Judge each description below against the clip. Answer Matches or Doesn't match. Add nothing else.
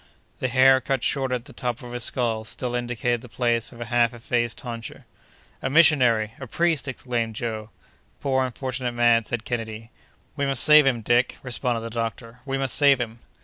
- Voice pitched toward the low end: Matches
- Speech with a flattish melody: Matches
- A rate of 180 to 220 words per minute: Matches